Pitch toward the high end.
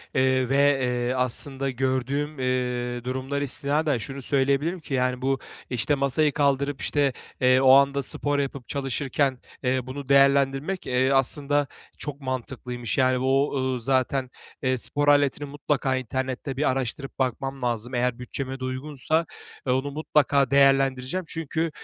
No: low, 135 Hz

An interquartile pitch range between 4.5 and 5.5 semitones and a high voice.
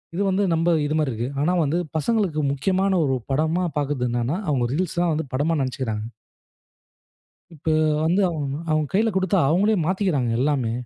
No: average, 5.2 semitones; medium, 155 Hz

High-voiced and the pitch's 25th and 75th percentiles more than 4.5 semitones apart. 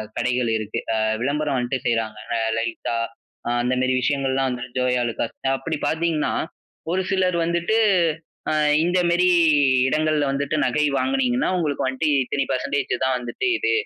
No: medium, 140 Hz; average, 5.1 semitones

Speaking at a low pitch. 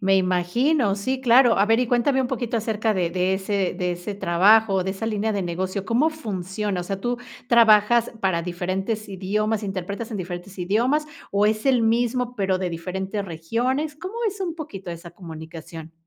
No: high, 205 Hz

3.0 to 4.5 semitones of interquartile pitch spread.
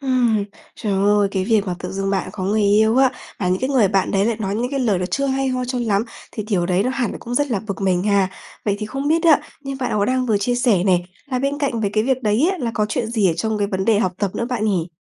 Yes: average, 4.2 semitones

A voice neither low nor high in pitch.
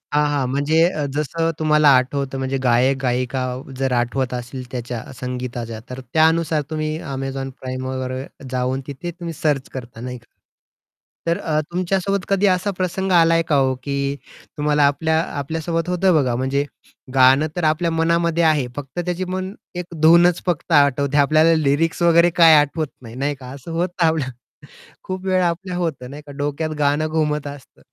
Yes: medium, 150 Hz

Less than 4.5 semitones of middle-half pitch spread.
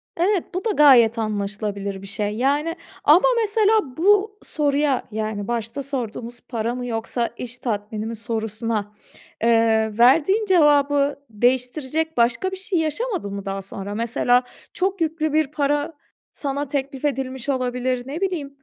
No: wide, 5.4 semitones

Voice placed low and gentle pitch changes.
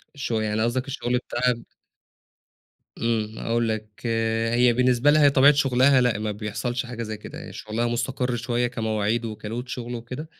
Yes: low, 120 Hz; narrow, 2.3 semitones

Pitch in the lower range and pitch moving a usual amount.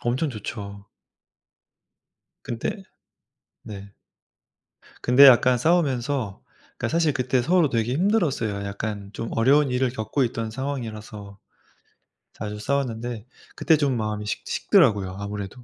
Yes: low, 120 Hz; average, 4.8 semitones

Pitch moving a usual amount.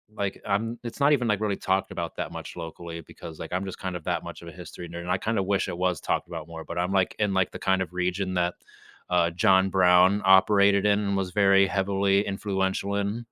No: narrow, 2.0 semitones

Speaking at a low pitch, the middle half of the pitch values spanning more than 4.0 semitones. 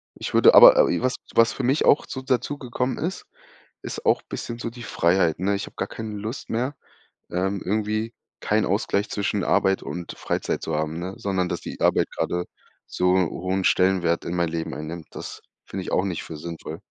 Yes: very low, 95 Hz; average, 4.9 semitones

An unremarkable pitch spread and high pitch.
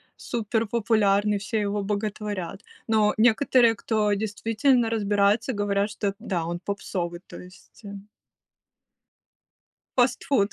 No: narrow, 2.0 semitones; high, 210 Hz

